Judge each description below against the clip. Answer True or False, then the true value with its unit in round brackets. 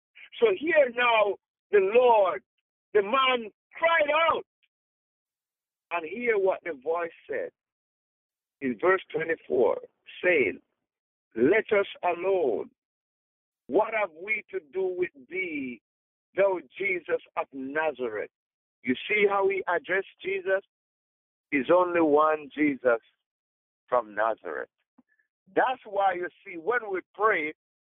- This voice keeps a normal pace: False (110 wpm)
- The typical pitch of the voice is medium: False (220 Hz)